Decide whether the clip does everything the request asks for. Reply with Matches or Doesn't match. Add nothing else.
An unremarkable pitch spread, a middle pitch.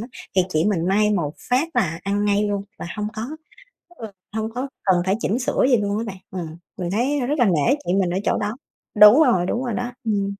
Doesn't match